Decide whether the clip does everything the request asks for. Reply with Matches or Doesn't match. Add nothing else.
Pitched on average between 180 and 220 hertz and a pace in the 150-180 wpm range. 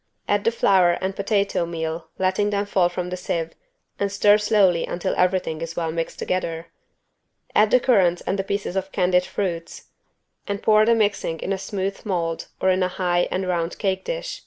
Doesn't match